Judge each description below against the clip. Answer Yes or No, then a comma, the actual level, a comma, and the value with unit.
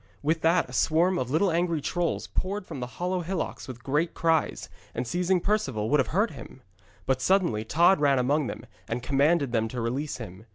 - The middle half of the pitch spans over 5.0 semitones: Yes, wide, 5.6 semitones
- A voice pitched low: No, medium, 150 Hz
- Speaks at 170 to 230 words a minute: Yes, average, 200 wpm